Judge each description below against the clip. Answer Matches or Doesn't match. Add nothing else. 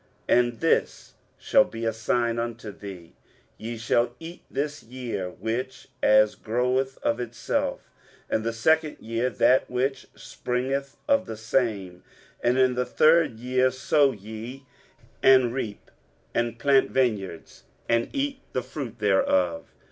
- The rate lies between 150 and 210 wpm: Doesn't match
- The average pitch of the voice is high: Doesn't match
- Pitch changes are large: Doesn't match